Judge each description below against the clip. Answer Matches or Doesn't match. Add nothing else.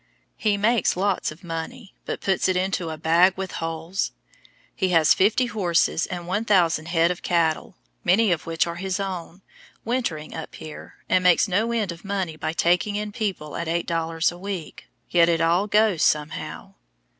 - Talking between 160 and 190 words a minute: Matches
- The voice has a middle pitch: Matches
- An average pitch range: Matches